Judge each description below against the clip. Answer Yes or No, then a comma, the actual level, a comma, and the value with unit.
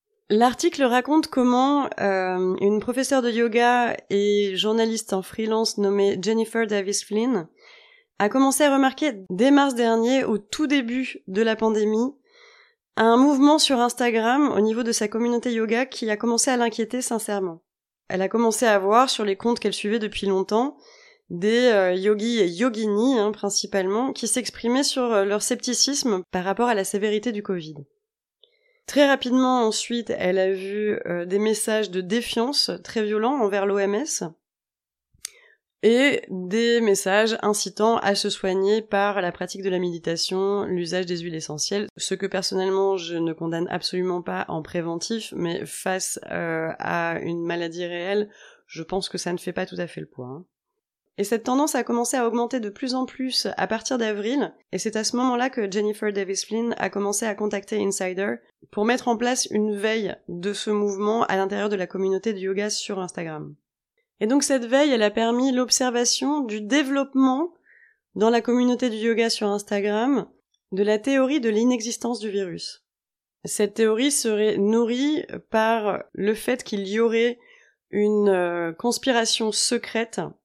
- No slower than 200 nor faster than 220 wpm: No, average, 165 wpm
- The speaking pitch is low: No, high, 220 Hz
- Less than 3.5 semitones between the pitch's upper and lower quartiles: No, average, 3.8 semitones